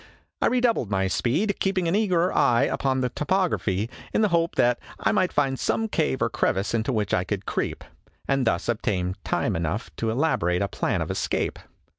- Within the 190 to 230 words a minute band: Yes, average, 195 wpm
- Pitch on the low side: Yes, low, 130 Hz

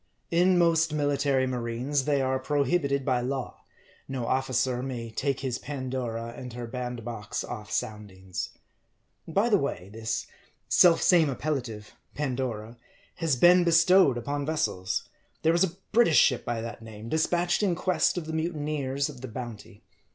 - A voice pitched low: Yes, low, 130 Hz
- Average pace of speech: Yes, average, 150 wpm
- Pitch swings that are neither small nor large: Yes, average, 5.0 semitones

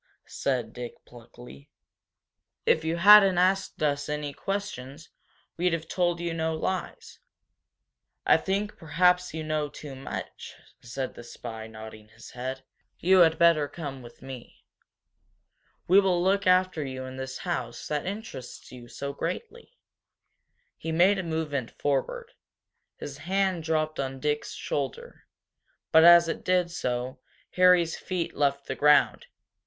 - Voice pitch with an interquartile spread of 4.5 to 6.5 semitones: Yes, average, 5.3 semitones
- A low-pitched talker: No, medium, 155 Hz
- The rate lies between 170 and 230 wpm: No, average, 140 wpm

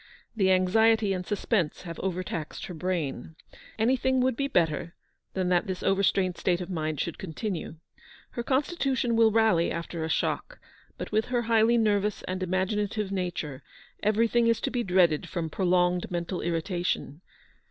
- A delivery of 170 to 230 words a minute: No, average, 155 wpm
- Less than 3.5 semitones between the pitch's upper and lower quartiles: No, average, 4.3 semitones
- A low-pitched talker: No, high, 190 Hz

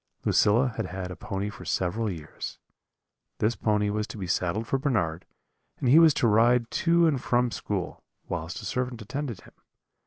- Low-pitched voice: Yes, low, 110 Hz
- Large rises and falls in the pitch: No, average, 4.4 semitones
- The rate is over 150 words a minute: Yes, average, 190 wpm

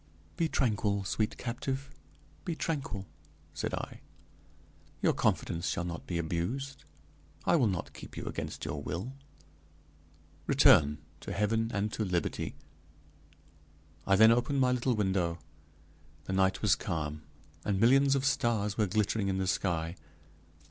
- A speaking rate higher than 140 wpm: No, slow, 135 wpm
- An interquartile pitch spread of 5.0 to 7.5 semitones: Yes, average, 5.3 semitones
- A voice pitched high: No, low, 105 Hz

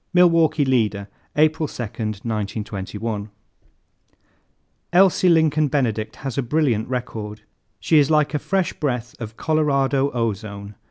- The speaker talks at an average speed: No, slow, 115 wpm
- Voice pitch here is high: No, low, 125 Hz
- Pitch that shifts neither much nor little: No, wide, 6.0 semitones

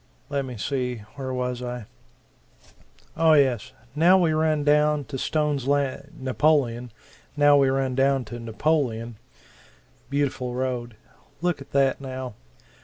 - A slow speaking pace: Yes, slow, 130 wpm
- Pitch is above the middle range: No, low, 135 Hz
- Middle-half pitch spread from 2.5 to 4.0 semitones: Yes, average, 2.8 semitones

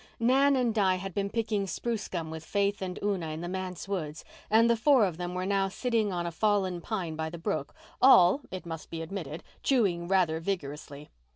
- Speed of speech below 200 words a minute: No, fast, 205 wpm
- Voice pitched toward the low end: No, high, 190 Hz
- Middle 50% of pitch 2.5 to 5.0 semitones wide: Yes, average, 3.9 semitones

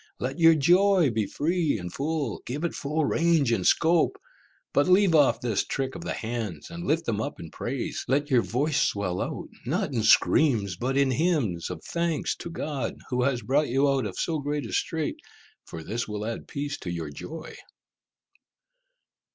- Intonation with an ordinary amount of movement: No, wide, 6.0 semitones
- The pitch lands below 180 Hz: Yes, medium, 140 Hz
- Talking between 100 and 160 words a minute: No, average, 185 wpm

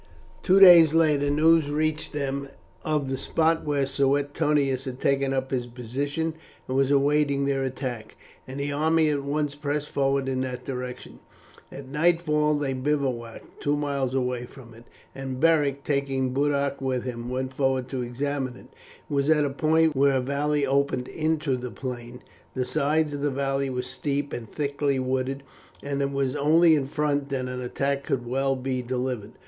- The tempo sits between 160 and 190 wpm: Yes, average, 175 wpm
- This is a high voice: No, medium, 140 Hz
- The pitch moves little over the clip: Yes, narrow, 2.1 semitones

